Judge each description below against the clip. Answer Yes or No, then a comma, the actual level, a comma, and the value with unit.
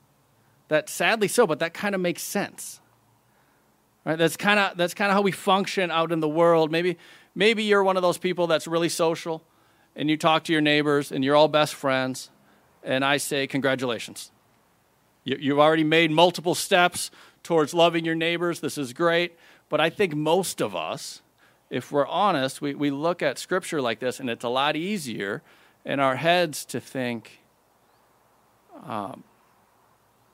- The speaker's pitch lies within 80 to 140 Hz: No, medium, 165 Hz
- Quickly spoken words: No, average, 175 wpm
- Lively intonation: No, average, 3.4 semitones